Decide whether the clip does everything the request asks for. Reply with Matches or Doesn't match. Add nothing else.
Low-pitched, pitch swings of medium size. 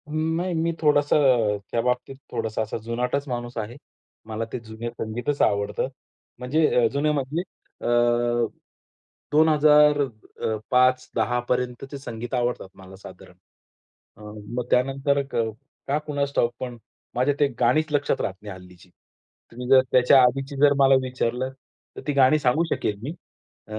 Matches